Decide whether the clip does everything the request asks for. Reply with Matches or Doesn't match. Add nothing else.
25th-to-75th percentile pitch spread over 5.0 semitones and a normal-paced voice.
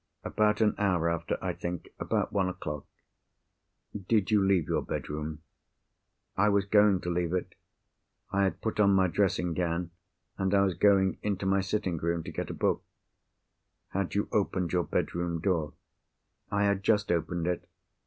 Doesn't match